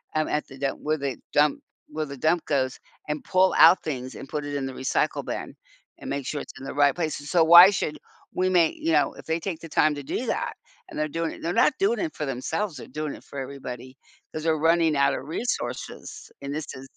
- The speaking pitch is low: No, medium, 150 Hz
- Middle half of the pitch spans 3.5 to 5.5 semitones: No, average, 3.0 semitones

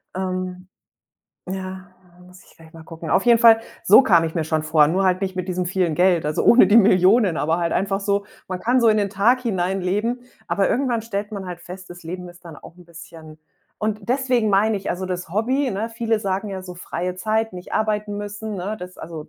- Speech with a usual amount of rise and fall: Yes, average, 3.4 semitones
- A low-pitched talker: No, high, 190 Hz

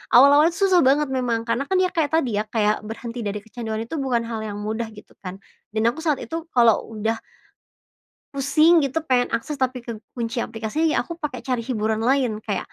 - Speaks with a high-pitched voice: Yes, high, 245 Hz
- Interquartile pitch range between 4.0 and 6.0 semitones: Yes, average, 4.5 semitones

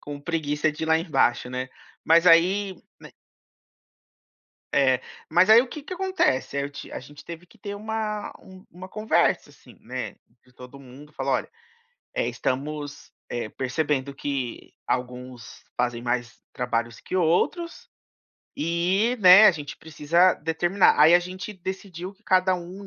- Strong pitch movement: Yes, wide, 5.7 semitones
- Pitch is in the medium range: Yes, medium, 165 Hz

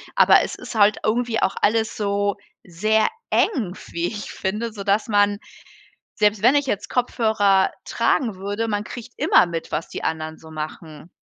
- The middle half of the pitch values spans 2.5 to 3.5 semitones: Yes, average, 2.9 semitones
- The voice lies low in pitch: No, high, 205 Hz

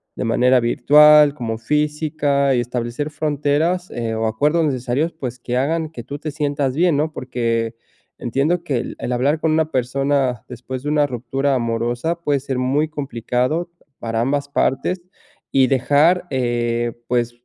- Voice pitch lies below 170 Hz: Yes, low, 135 Hz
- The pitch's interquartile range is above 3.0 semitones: Yes, average, 3.7 semitones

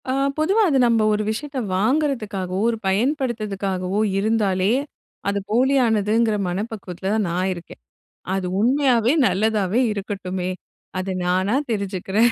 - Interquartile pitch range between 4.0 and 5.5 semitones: No, average, 3.6 semitones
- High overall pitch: Yes, high, 210 Hz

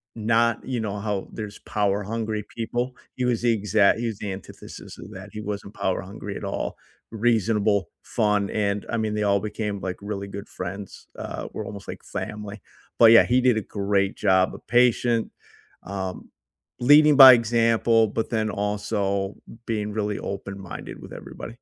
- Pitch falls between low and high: No, low, 105 Hz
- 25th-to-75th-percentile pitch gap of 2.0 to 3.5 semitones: Yes, narrow, 2.4 semitones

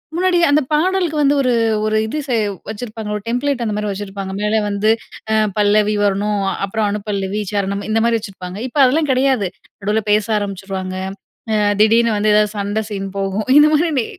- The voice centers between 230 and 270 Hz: No, high, 215 Hz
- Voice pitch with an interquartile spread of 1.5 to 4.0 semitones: Yes, average, 3.6 semitones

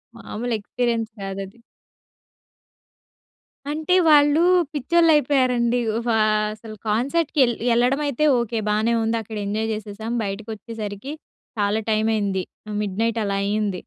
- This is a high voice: Yes, high, 225 Hz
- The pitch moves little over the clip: No, average, 3.2 semitones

